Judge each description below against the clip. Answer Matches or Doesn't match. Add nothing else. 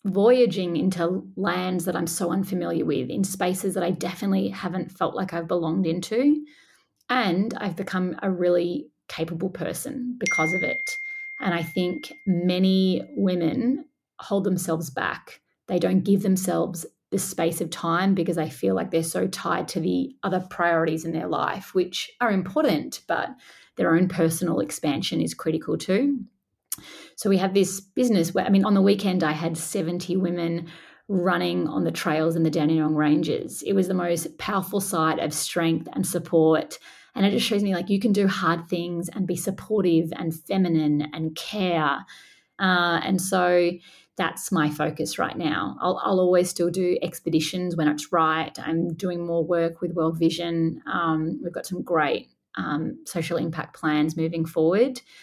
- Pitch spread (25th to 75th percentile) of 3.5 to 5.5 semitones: Doesn't match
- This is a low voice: Doesn't match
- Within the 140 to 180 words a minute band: Matches